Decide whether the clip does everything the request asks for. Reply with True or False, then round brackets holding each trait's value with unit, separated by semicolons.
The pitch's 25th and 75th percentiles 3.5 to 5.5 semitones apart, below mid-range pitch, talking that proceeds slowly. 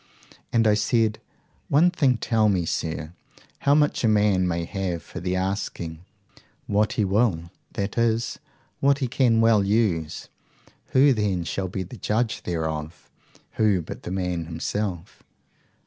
False (4.5 semitones; 100 Hz; 150 wpm)